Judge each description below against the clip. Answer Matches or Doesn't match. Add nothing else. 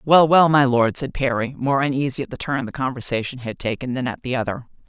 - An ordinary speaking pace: Doesn't match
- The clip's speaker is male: Doesn't match